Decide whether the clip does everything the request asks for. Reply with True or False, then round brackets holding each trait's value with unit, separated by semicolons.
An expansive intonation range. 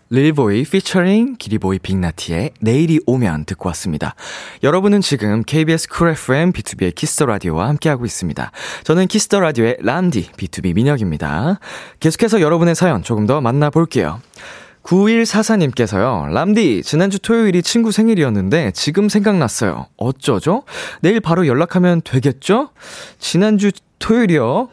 True (7.8 semitones)